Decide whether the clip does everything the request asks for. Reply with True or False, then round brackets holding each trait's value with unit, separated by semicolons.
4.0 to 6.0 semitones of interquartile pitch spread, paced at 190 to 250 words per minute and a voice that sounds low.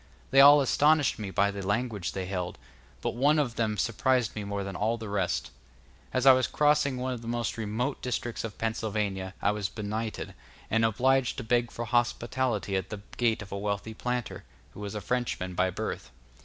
False (3.6 semitones; 195 wpm; 110 Hz)